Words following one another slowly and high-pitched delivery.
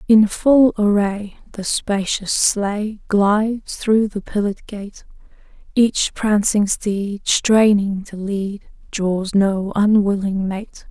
Yes: slow, 115 wpm; high, 205 Hz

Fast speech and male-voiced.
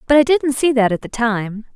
No: fast, 275 wpm; female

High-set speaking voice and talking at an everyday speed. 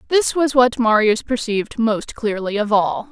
Yes: high, 225 Hz; average, 175 wpm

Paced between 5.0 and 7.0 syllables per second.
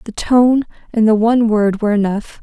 Yes: 5.4 syllables/s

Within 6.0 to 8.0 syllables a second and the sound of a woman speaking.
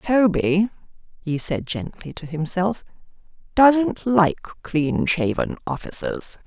No: 3.6 syllables/s; female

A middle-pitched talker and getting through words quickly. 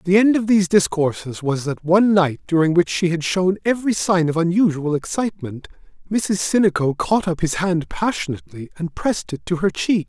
No: medium, 180 Hz; average, 190 wpm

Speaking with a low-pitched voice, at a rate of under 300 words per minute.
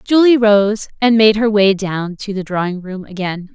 No: high, 205 Hz; fast, 205 wpm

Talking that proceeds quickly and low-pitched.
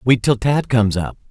Yes: fast, 230 wpm; low, 120 Hz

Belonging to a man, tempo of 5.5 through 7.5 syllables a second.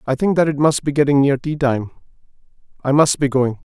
Yes: male; 5.7 syllables/s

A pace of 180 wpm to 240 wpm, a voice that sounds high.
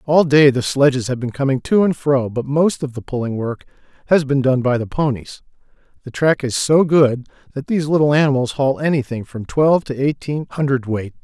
No: fast, 205 wpm; low, 135 Hz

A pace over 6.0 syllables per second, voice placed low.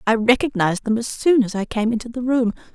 No: 6.2 syllables/s; high, 230 Hz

